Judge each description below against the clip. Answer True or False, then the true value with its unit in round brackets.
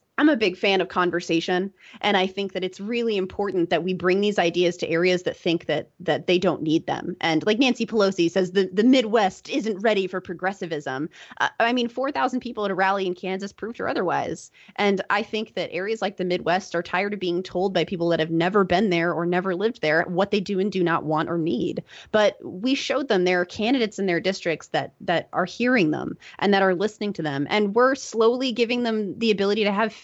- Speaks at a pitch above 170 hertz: True (190 Hz)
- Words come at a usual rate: False (230 wpm)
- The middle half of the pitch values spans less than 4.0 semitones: True (3.3 semitones)